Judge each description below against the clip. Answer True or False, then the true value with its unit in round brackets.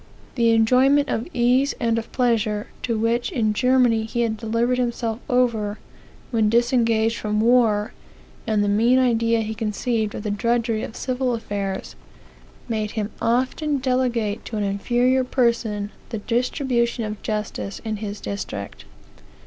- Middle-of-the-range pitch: False (230 Hz)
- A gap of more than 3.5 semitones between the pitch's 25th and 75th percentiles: False (2.5 semitones)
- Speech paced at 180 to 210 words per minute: False (145 wpm)